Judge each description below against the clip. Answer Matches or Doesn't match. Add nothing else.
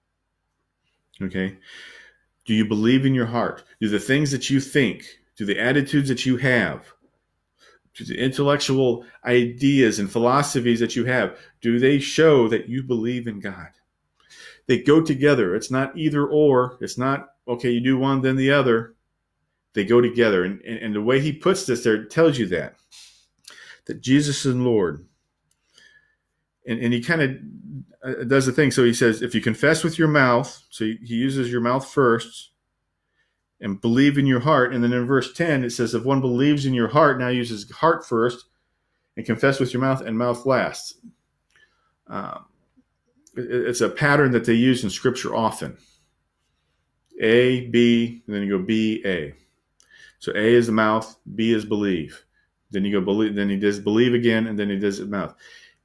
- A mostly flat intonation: Doesn't match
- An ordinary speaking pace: Matches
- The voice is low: Matches